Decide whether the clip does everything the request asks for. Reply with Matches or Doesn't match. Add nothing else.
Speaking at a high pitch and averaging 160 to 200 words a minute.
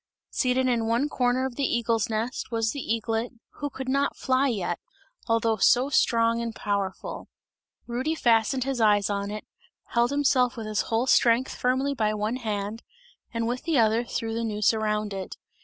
Matches